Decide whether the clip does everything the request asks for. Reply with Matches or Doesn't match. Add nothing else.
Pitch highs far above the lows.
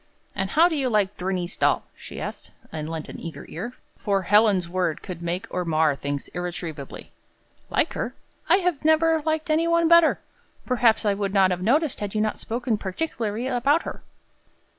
Matches